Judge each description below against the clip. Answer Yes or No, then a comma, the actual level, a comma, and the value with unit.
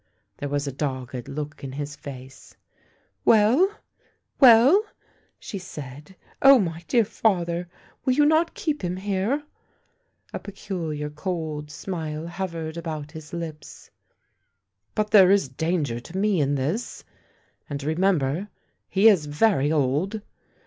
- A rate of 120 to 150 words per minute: Yes, average, 145 wpm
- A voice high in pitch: No, medium, 165 Hz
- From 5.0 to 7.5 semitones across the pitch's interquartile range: Yes, wide, 5.5 semitones